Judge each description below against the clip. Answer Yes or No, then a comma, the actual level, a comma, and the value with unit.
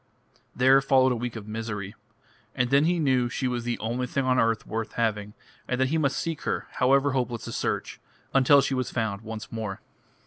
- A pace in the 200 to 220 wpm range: Yes, fast, 205 wpm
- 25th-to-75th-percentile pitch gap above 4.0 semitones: No, average, 3.1 semitones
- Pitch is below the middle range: Yes, low, 125 Hz